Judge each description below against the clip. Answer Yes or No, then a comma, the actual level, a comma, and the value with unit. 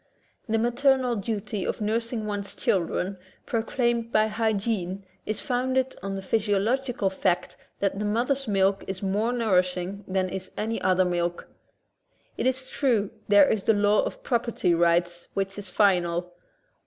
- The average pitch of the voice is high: Yes, high, 205 Hz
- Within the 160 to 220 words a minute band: No, average, 145 wpm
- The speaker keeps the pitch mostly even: No, average, 3.4 semitones